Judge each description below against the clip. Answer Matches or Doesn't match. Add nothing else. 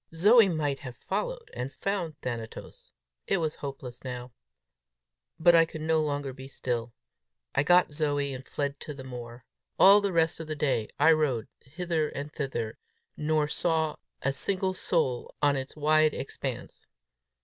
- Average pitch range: Matches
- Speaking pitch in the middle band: Matches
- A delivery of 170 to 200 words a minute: Doesn't match